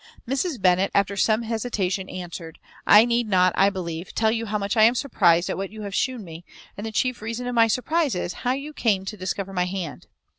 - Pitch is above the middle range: Yes, high, 205 Hz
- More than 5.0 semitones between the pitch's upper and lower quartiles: No, average, 4.0 semitones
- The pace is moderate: No, fast, 225 wpm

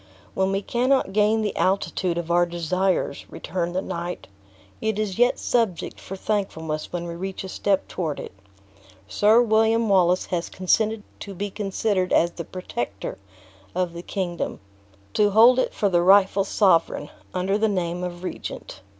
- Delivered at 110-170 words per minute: Yes, average, 160 wpm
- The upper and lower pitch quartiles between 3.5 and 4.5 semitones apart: No, average, 3.1 semitones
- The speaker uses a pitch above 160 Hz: Yes, high, 190 Hz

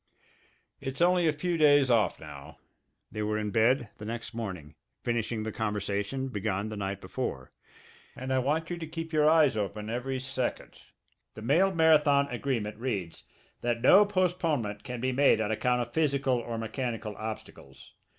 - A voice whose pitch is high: No, low, 125 Hz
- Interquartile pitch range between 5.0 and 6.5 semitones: Yes, wide, 5.4 semitones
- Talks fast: No, average, 165 wpm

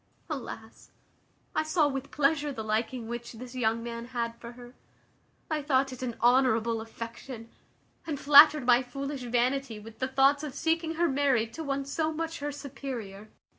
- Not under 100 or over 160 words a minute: No, average, 170 wpm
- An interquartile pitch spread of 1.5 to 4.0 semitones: Yes, average, 3.6 semitones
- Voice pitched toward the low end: No, very high, 260 Hz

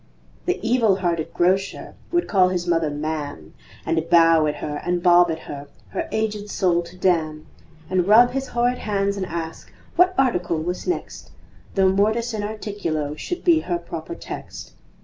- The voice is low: No, medium, 180 Hz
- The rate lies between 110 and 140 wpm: No, average, 170 wpm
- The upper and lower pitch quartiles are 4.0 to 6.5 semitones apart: Yes, average, 4.4 semitones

